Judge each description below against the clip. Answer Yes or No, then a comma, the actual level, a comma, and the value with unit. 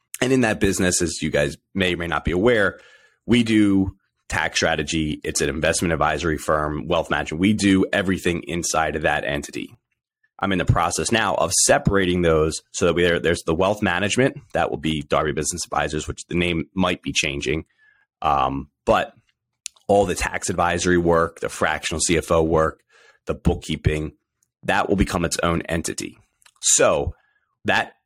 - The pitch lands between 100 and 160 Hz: No, very low, 85 Hz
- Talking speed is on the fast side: No, average, 170 wpm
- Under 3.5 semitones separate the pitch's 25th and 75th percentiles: No, average, 3.8 semitones